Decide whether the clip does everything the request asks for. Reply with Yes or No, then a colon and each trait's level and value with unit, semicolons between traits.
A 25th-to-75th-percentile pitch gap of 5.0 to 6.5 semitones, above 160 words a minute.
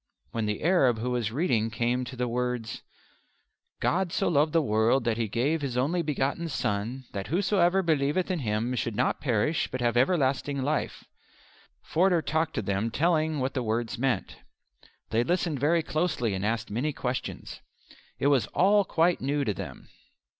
Yes: wide, 5.5 semitones; average, 170 wpm